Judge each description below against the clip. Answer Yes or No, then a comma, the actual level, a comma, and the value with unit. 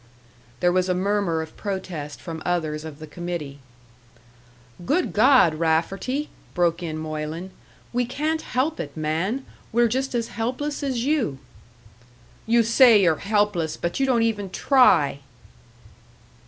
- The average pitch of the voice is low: No, high, 190 Hz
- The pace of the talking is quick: No, slow, 135 wpm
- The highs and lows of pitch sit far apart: Yes, wide, 7.4 semitones